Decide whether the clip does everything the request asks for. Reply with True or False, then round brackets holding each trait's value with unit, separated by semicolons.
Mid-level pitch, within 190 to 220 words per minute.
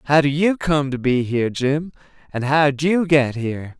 True (145 Hz; 205 wpm)